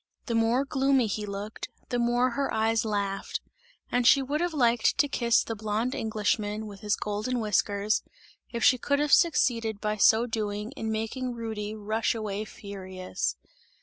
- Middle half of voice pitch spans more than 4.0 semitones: No, average, 2.8 semitones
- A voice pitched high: Yes, high, 220 Hz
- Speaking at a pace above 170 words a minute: No, average, 165 wpm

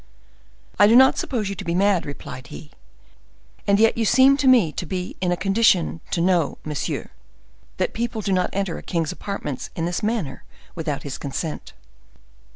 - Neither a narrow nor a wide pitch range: Yes, average, 4.8 semitones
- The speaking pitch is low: No, medium, 185 Hz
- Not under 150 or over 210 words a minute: Yes, average, 180 wpm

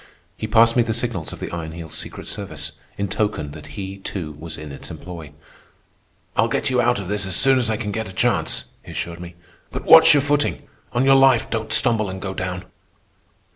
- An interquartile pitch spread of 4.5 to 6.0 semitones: Yes, wide, 5.4 semitones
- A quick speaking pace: Yes, fast, 215 wpm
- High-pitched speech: No, low, 105 Hz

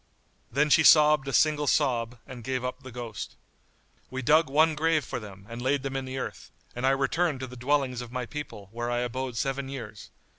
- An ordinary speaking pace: No, fast, 215 wpm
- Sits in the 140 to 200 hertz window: No, low, 130 Hz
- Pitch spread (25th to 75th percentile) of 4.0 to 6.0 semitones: No, average, 3.1 semitones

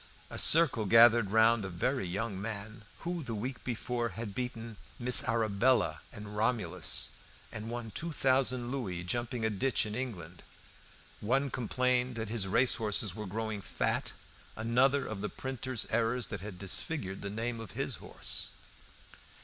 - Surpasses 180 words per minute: No, average, 150 wpm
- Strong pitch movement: No, average, 3.2 semitones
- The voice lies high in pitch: No, low, 115 Hz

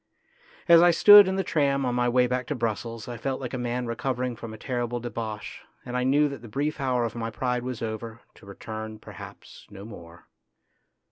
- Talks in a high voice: No, low, 120 Hz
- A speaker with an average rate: No, fast, 210 wpm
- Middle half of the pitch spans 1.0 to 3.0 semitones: Yes, average, 2.7 semitones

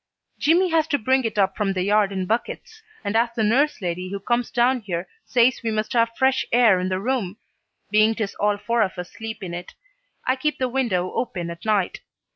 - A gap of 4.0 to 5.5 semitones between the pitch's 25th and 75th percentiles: Yes, average, 4.6 semitones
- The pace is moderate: No, fast, 220 wpm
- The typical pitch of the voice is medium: No, high, 220 Hz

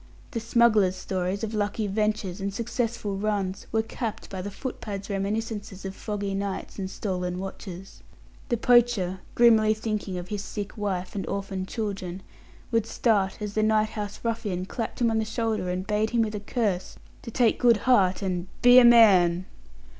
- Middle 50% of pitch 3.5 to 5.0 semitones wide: No, average, 2.7 semitones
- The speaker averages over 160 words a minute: Yes, average, 175 wpm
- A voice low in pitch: No, high, 205 Hz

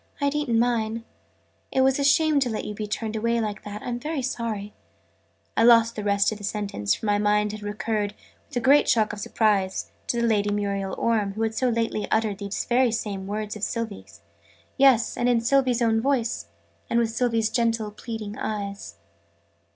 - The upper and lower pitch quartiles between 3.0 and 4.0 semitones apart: No, narrow, 2.4 semitones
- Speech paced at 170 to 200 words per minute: Yes, average, 190 wpm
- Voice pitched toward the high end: Yes, high, 220 Hz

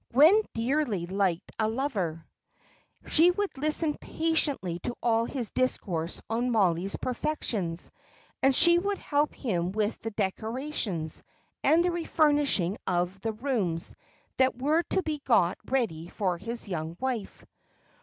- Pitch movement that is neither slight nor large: No, wide, 7.9 semitones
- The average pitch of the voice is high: Yes, high, 230 Hz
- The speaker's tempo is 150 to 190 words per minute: No, slow, 135 wpm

